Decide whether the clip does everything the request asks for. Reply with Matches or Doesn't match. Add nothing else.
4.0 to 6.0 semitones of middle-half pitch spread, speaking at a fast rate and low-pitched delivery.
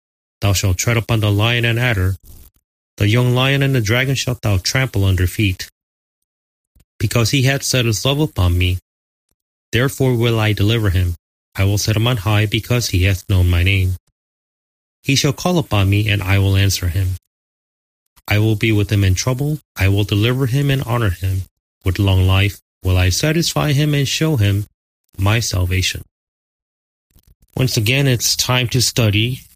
Doesn't match